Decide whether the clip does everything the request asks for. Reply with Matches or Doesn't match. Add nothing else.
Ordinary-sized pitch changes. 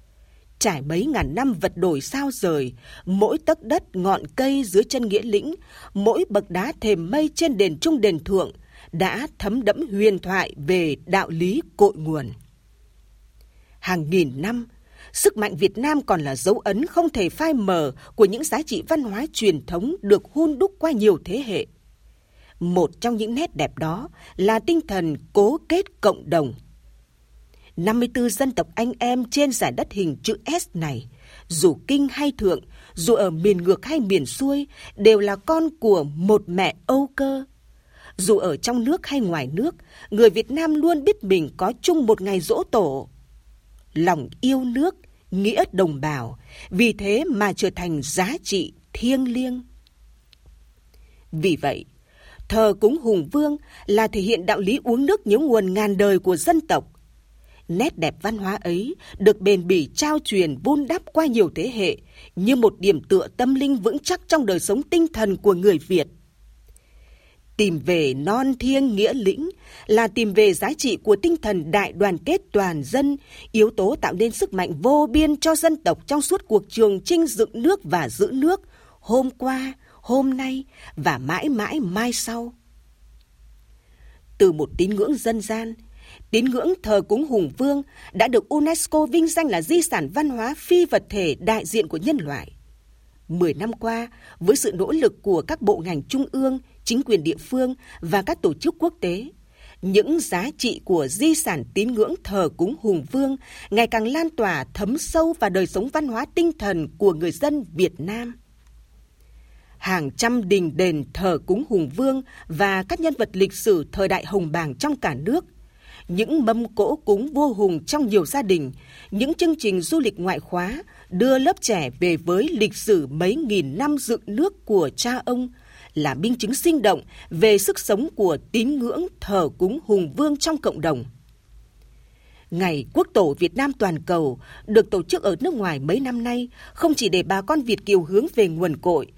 Doesn't match